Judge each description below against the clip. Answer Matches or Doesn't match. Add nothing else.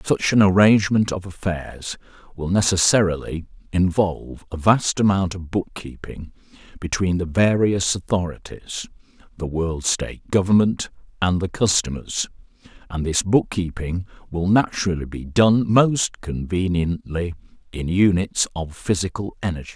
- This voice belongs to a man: Matches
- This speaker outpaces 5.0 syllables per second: Doesn't match